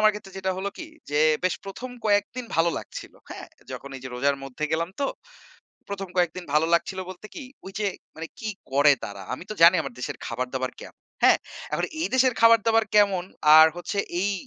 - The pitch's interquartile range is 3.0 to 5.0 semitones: No, wide, 5.5 semitones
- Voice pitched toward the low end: No, medium, 185 Hz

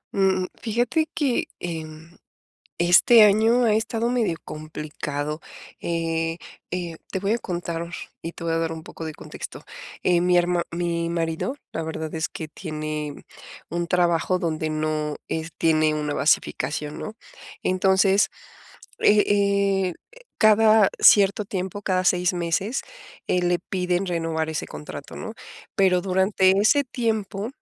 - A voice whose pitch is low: No, medium, 175 Hz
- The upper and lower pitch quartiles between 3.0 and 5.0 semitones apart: Yes, average, 3.6 semitones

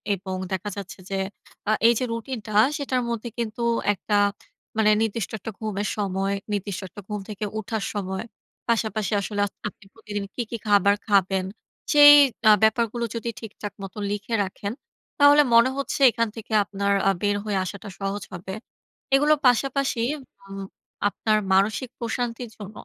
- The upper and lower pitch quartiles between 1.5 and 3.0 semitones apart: Yes, average, 2.7 semitones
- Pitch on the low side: No, high, 210 Hz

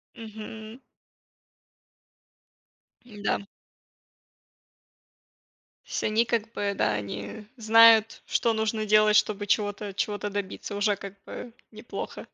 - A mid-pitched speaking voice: No, high, 215 Hz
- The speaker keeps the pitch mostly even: Yes, narrow, 1.5 semitones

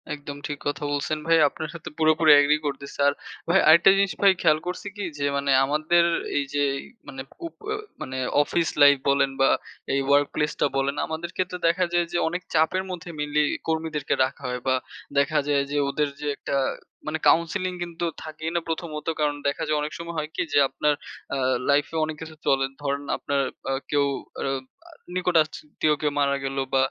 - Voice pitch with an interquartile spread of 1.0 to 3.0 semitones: Yes, narrow, 2.5 semitones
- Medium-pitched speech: Yes, medium, 150 Hz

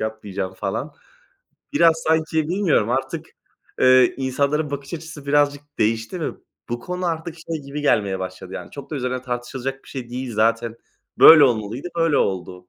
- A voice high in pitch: No, low, 130 Hz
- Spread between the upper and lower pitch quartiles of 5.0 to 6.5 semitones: Yes, wide, 5.5 semitones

